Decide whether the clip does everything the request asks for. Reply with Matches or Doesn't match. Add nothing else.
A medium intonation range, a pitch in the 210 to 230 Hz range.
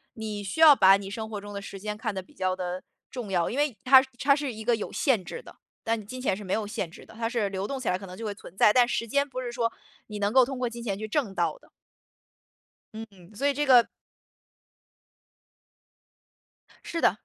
Matches